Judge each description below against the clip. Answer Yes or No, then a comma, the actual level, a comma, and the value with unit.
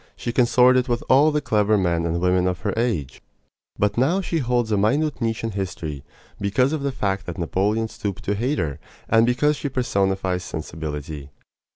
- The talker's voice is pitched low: Yes, low, 105 Hz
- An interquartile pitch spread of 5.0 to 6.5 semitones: Yes, wide, 5.6 semitones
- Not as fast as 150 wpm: No, average, 185 wpm